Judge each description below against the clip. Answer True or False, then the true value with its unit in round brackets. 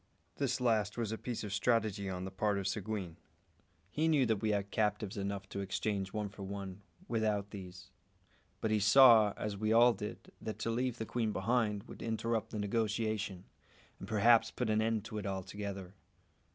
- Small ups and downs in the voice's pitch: True (2.2 semitones)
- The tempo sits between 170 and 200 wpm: True (185 wpm)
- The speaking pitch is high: False (105 Hz)